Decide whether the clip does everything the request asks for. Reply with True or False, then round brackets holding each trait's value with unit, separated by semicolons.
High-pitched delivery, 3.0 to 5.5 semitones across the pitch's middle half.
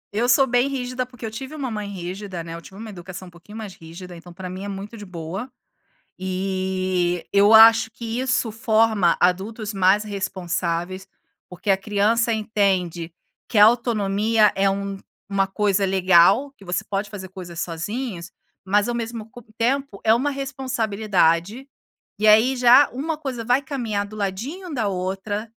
True (205 Hz; 3.7 semitones)